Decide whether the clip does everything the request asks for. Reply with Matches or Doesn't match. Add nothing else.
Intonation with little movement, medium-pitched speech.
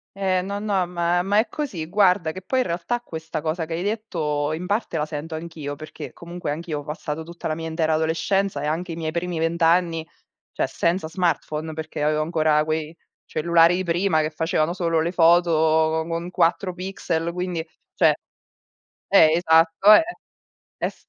Matches